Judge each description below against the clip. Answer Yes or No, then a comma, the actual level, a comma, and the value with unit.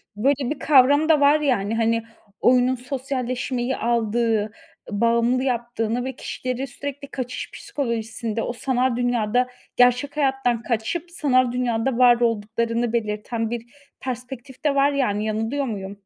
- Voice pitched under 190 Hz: No, high, 245 Hz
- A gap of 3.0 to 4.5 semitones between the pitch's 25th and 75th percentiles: No, narrow, 2.6 semitones